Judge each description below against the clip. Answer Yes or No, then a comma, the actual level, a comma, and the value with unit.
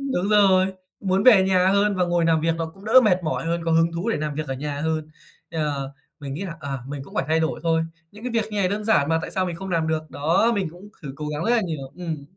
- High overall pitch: No, medium, 165 Hz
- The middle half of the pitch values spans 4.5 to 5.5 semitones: No, average, 3.7 semitones